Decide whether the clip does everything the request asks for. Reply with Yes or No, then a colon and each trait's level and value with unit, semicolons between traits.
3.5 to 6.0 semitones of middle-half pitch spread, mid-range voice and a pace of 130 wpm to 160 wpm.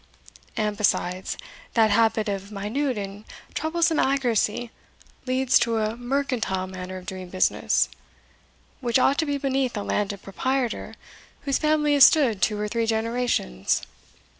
No: average, 4.8 semitones; high, 230 Hz; average, 140 wpm